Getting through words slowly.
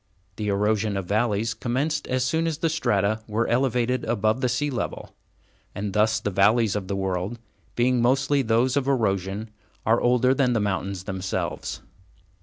No: average, 165 wpm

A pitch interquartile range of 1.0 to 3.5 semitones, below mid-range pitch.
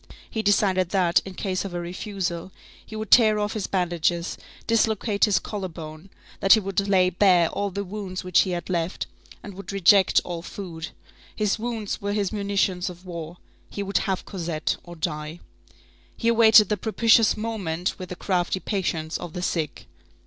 No: average, 2.9 semitones; high, 190 Hz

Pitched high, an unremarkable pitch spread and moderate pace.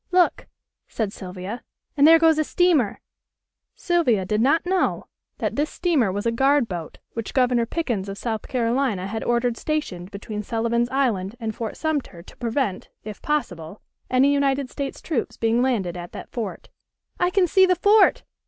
No: high, 240 Hz; wide, 6.0 semitones; average, 170 wpm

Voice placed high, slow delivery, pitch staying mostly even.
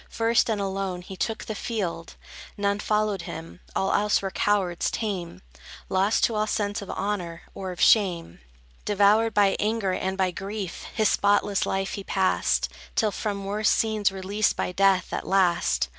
No: high, 200 Hz; average, 165 wpm; narrow, 1.9 semitones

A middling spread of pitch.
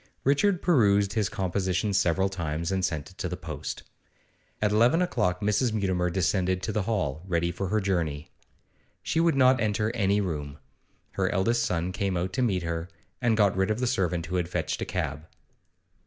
Yes: average, 3.5 semitones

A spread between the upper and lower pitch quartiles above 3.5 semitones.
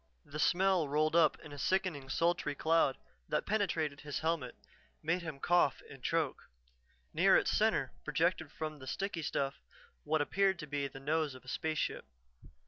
No: average, 2.9 semitones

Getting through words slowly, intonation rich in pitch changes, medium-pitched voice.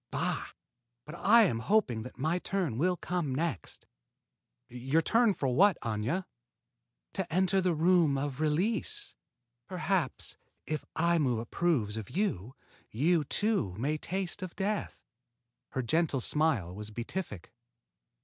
Yes: slow, 130 wpm; wide, 6.7 semitones; medium, 160 Hz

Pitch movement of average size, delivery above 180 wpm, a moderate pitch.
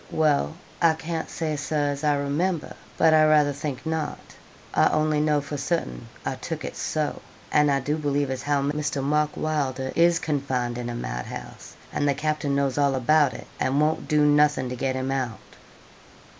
No: narrow, 2.2 semitones; average, 190 wpm; medium, 145 Hz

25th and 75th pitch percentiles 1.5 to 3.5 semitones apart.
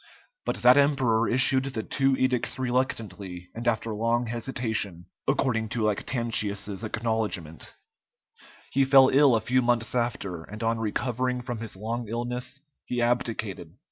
Yes: average, 2.7 semitones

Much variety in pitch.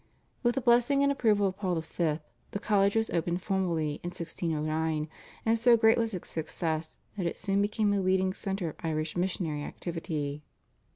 No: average, 4.6 semitones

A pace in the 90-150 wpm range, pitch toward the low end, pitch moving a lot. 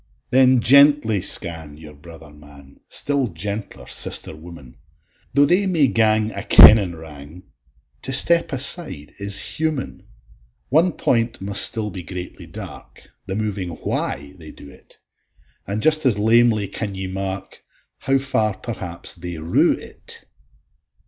Yes: slow, 135 wpm; low, 100 Hz; wide, 7.1 semitones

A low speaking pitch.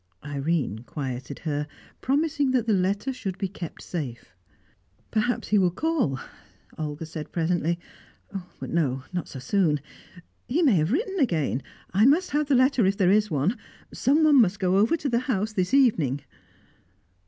No: high, 195 Hz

